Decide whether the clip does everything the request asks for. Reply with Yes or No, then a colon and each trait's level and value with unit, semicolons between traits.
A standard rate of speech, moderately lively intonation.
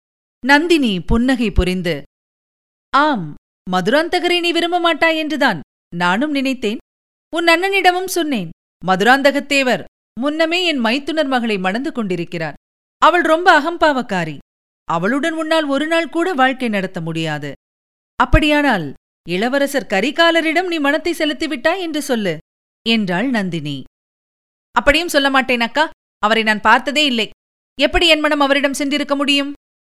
No: average, 110 wpm; wide, 8.4 semitones